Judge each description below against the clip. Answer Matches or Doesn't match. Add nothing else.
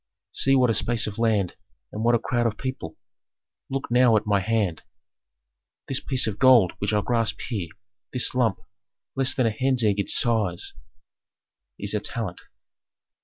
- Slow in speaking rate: Doesn't match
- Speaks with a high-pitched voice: Doesn't match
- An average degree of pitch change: Matches